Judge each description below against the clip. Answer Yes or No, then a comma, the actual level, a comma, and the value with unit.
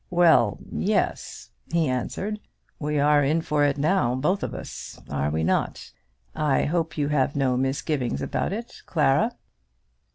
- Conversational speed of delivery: Yes, average, 150 wpm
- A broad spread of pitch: No, average, 3.8 semitones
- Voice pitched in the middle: Yes, medium, 145 Hz